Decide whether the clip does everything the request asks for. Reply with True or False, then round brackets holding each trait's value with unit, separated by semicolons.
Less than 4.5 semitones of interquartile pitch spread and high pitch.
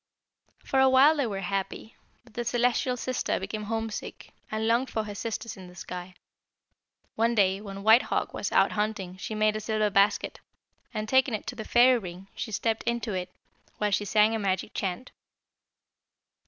True (3.1 semitones; 215 Hz)